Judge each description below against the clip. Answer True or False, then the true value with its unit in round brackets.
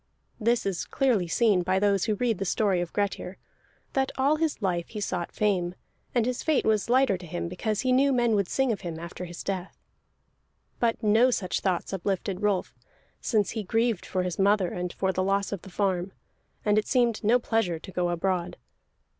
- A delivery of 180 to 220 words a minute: True (200 wpm)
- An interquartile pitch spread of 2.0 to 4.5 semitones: True (4.0 semitones)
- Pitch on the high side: True (200 Hz)